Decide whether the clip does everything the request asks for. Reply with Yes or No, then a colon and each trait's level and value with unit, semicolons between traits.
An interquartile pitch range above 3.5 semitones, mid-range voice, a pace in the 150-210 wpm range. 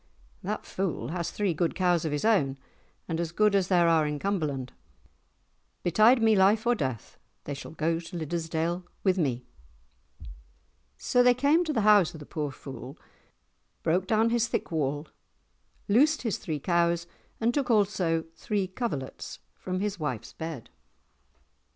Yes: average, 5.3 semitones; medium, 175 Hz; average, 155 wpm